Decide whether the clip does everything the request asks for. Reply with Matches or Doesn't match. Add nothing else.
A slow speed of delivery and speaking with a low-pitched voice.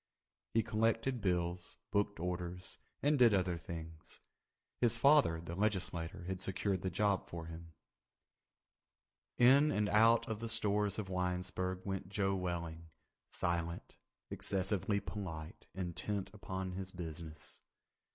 Matches